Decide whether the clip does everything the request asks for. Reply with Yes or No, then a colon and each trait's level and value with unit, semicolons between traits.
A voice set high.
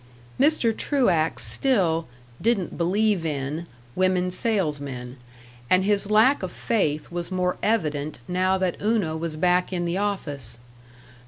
No: medium, 180 Hz